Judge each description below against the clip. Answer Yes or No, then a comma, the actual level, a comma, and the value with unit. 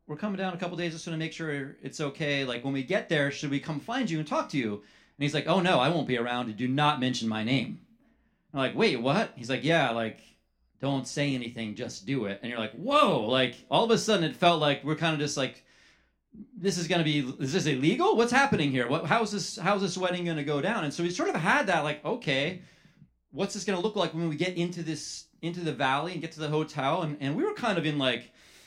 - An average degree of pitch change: Yes, average, 4.9 semitones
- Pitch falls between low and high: Yes, medium, 155 Hz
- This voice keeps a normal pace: No, fast, 265 wpm